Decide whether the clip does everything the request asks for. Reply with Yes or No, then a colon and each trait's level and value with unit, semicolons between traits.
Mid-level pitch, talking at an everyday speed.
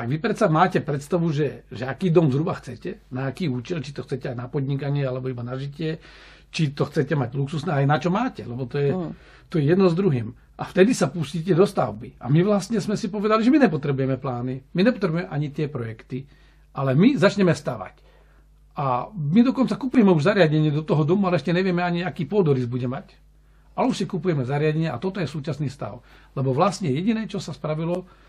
No: medium, 155 Hz; fast, 210 wpm